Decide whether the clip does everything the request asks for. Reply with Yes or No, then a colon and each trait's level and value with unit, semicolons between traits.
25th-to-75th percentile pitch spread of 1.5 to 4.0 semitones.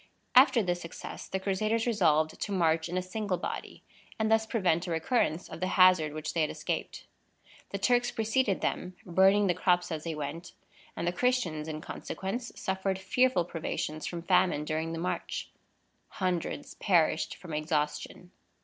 Yes: average, 3.7 semitones